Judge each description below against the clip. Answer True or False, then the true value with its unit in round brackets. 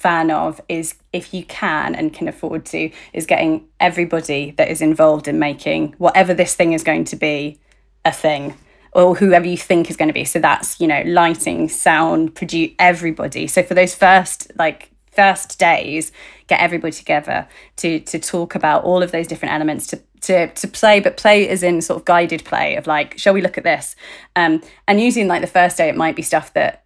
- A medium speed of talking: False (210 wpm)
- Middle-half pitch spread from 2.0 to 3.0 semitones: True (2.7 semitones)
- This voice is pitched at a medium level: True (175 Hz)